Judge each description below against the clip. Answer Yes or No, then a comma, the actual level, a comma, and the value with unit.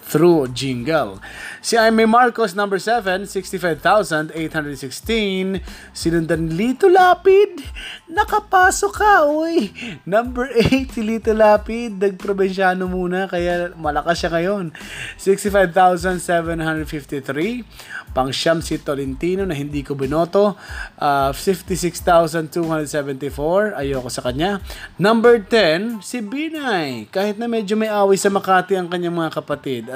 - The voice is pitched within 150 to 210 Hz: Yes, medium, 185 Hz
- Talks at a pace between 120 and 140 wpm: No, slow, 110 wpm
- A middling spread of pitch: No, wide, 5.9 semitones